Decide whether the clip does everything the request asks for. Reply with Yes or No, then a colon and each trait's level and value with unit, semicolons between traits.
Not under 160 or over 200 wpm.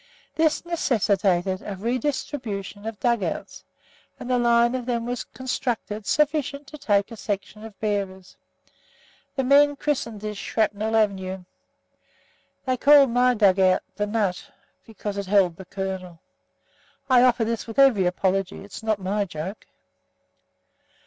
No: average, 140 wpm